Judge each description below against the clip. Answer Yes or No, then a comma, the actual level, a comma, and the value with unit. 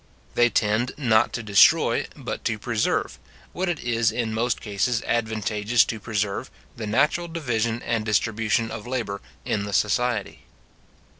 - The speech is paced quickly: No, average, 145 wpm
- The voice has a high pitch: No, low, 115 Hz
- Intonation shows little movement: Yes, narrow, 2.1 semitones